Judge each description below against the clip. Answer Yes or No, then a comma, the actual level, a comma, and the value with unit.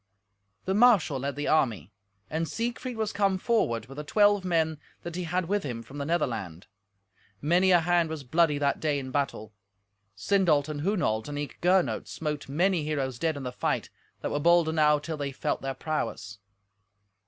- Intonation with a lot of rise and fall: No, average, 4.3 semitones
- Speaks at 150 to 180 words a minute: No, average, 190 wpm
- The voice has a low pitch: No, medium, 155 Hz